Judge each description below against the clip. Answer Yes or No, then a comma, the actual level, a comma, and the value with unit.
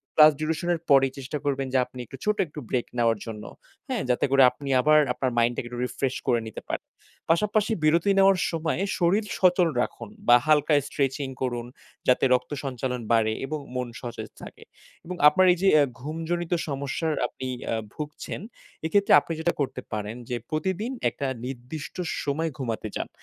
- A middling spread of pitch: Yes, average, 4.6 semitones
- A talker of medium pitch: Yes, medium, 145 Hz